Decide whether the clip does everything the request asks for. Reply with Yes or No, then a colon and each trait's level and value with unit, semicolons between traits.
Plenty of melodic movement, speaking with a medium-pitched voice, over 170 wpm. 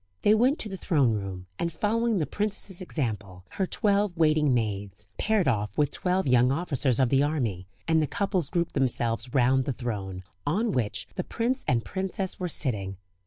Yes: wide, 8.6 semitones; medium, 145 Hz; average, 180 wpm